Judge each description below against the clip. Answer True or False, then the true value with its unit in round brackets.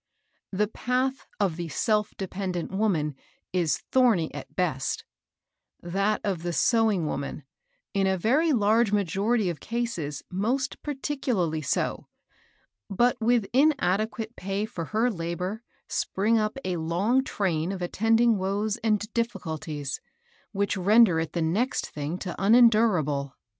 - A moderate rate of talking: False (130 wpm)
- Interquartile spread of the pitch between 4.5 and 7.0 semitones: True (4.8 semitones)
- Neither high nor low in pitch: False (200 Hz)